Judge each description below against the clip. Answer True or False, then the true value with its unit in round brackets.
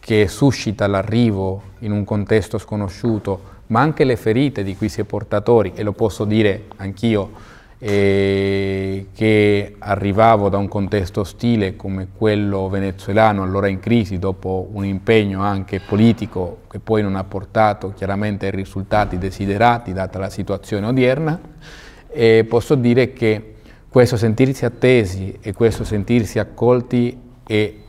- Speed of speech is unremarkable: True (140 wpm)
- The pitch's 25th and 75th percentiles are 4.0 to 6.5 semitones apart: False (2.7 semitones)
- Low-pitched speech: True (105 Hz)